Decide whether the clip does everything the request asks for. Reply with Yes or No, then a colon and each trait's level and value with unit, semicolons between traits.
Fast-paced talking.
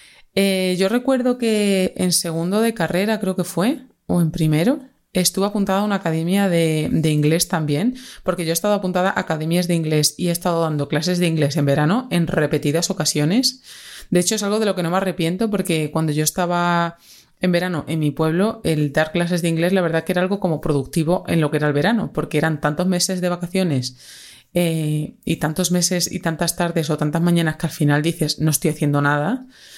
Yes: fast, 210 wpm